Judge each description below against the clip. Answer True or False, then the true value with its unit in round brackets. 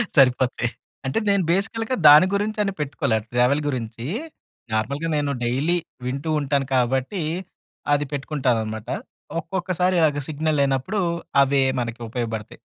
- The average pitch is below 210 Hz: True (140 Hz)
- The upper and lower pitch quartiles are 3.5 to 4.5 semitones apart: False (4.9 semitones)